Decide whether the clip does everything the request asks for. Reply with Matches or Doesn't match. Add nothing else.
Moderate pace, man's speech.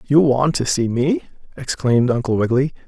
Matches